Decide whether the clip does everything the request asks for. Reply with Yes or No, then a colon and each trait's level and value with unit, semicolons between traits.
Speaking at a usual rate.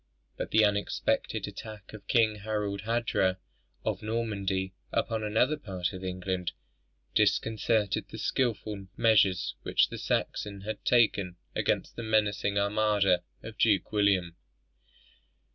No: slow, 120 wpm